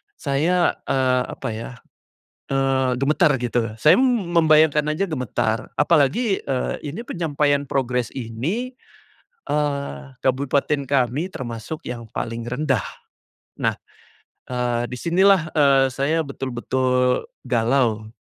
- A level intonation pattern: No, average, 3.8 semitones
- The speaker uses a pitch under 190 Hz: Yes, low, 135 Hz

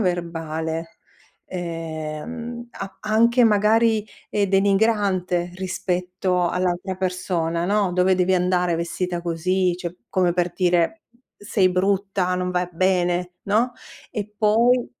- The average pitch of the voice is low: No, medium, 185 Hz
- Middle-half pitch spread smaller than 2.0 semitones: No, narrow, 2.5 semitones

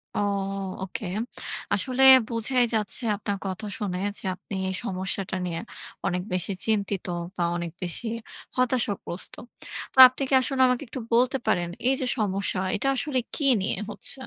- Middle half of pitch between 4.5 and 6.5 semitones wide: Yes, average, 5.1 semitones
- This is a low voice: No, high, 205 Hz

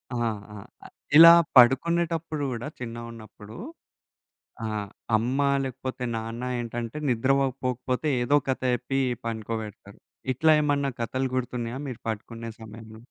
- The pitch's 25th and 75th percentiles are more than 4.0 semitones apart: No, average, 2.9 semitones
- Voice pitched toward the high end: No, low, 120 Hz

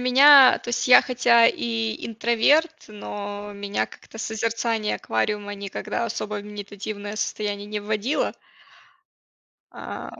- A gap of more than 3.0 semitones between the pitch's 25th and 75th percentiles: No, narrow, 2.5 semitones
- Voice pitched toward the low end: No, high, 215 Hz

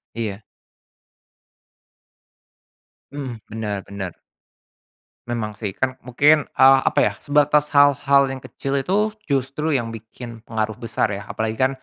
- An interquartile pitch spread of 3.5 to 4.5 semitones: Yes, average, 4.2 semitones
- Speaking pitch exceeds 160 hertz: No, low, 125 Hz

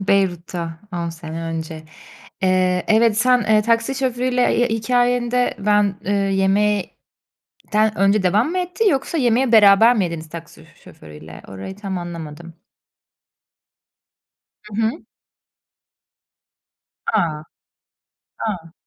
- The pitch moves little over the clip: No, wide, 5.6 semitones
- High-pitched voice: Yes, high, 200 Hz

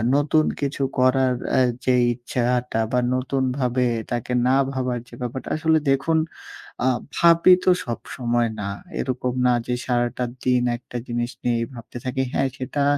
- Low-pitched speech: Yes, low, 125 Hz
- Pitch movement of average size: No, narrow, 1.7 semitones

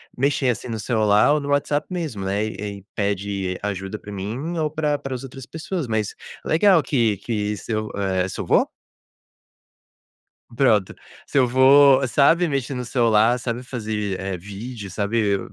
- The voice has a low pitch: Yes, low, 115 Hz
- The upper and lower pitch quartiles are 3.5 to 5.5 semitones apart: Yes, average, 5.1 semitones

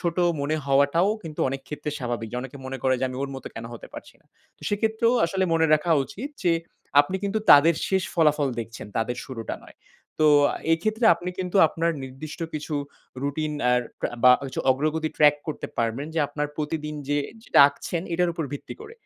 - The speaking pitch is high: No, medium, 150 Hz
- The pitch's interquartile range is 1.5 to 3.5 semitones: No, average, 4.1 semitones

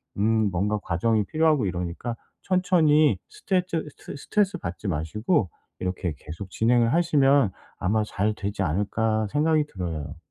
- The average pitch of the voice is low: Yes, low, 110 Hz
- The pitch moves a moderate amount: No, wide, 8.6 semitones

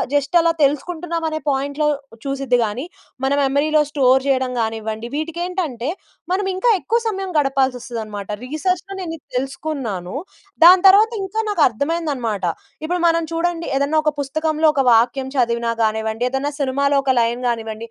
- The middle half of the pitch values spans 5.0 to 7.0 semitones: Yes, average, 5.3 semitones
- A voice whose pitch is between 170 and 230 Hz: No, very high, 280 Hz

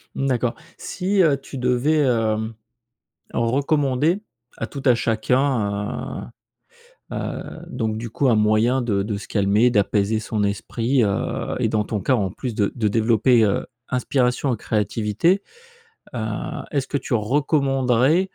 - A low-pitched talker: Yes, low, 120 Hz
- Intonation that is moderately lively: Yes, average, 4.0 semitones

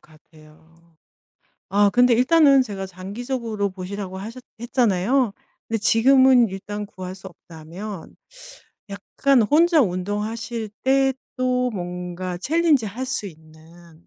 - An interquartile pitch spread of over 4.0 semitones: Yes, wide, 5.6 semitones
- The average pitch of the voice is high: Yes, high, 205 Hz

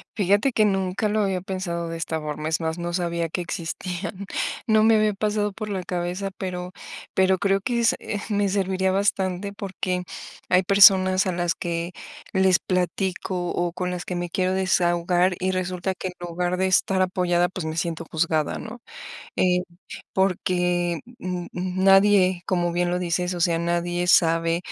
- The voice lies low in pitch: No, medium, 180 Hz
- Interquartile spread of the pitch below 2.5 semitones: Yes, narrow, 1.6 semitones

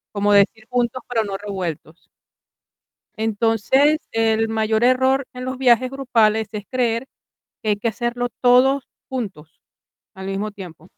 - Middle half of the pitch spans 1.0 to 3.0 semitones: No, average, 3.5 semitones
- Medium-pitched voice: No, high, 225 Hz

